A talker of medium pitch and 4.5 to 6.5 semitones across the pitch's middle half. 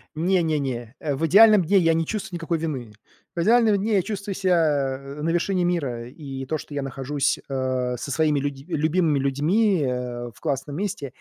Yes: medium, 150 Hz; average, 4.8 semitones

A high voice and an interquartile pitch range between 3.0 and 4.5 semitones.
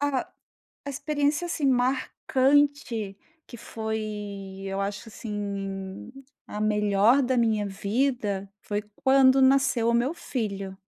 No: high, 225 Hz; average, 4.9 semitones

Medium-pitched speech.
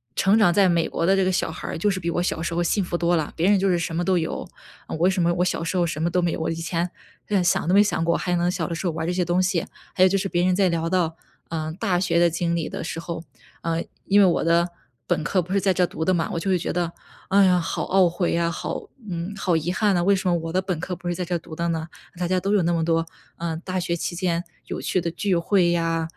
Yes: medium, 175 Hz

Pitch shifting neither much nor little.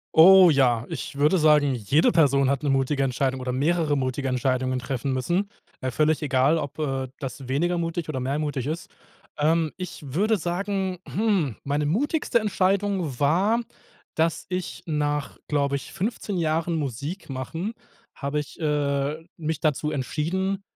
Yes: average, 4.1 semitones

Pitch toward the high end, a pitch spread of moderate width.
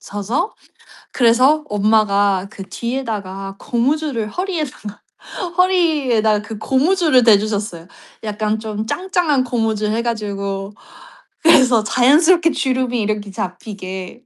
Yes: high, 225 Hz; average, 4.6 semitones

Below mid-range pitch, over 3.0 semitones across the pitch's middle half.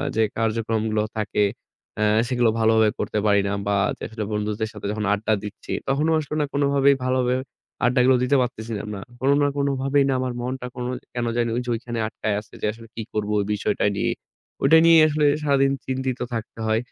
Yes: low, 120 Hz; average, 3.7 semitones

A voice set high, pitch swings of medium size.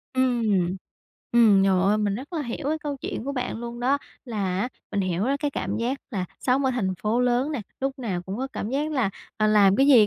Yes: high, 235 Hz; average, 4.9 semitones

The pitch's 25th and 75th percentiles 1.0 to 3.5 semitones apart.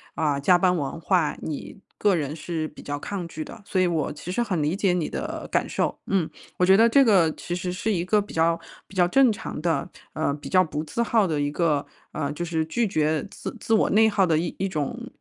No: average, 3.9 semitones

